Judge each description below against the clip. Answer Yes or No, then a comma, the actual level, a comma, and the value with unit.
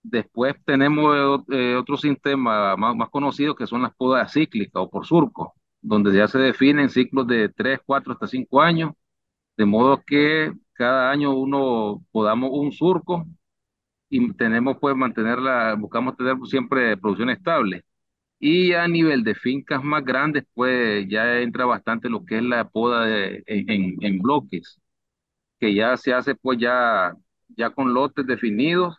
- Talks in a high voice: No, low, 130 Hz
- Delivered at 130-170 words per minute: Yes, average, 155 wpm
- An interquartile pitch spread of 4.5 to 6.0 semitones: No, average, 3.2 semitones